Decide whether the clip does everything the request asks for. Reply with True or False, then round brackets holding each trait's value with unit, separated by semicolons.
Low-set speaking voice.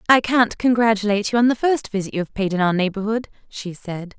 False (210 Hz)